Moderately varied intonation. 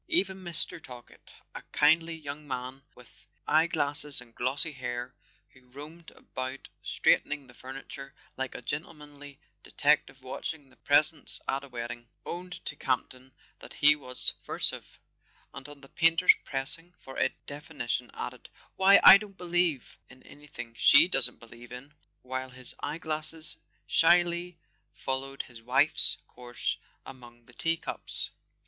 Yes: average, 4.0 semitones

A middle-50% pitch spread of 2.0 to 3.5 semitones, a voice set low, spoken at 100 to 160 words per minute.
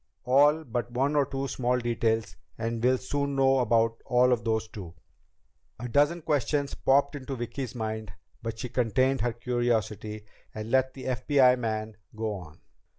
Yes: average, 3.1 semitones; low, 125 Hz; average, 155 wpm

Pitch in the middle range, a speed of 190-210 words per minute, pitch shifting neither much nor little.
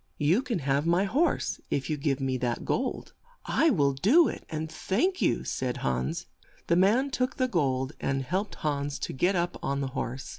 No: medium, 155 Hz; average, 195 wpm; wide, 7.0 semitones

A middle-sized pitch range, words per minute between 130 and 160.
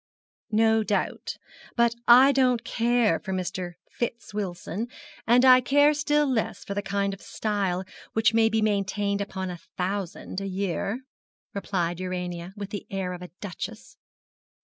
Yes: average, 3.8 semitones; average, 150 wpm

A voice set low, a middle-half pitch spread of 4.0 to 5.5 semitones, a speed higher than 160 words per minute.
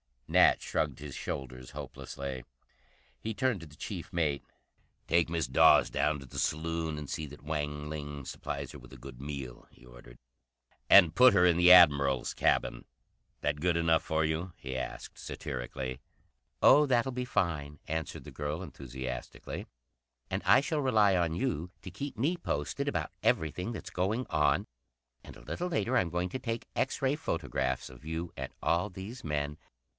Yes: very low, 80 Hz; average, 5.1 semitones; average, 170 wpm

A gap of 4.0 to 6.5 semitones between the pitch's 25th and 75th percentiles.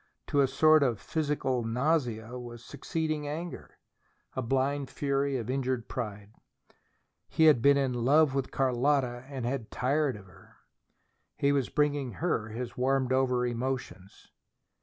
No: average, 2.8 semitones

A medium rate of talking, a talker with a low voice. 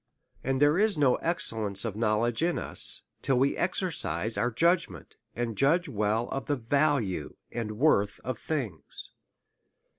Yes: average, 150 wpm; low, 125 Hz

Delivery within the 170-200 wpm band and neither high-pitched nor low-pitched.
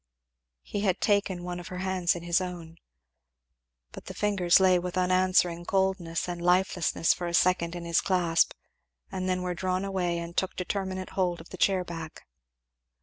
Yes: average, 175 wpm; medium, 180 Hz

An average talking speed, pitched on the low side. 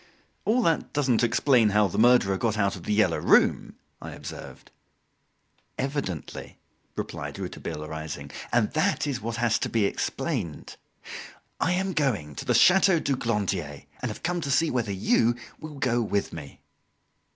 Yes: average, 160 wpm; low, 115 Hz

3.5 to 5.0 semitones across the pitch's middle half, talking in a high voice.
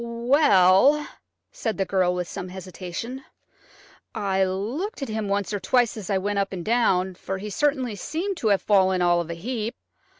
Yes: average, 4.4 semitones; high, 200 Hz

